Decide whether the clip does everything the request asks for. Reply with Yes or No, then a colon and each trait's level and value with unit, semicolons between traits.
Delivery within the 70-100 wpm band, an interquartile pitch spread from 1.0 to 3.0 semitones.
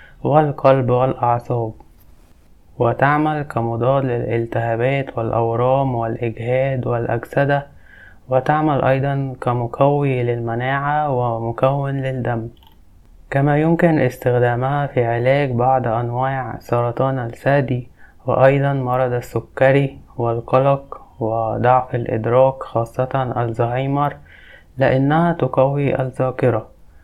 Yes: average, 75 wpm; average, 2.7 semitones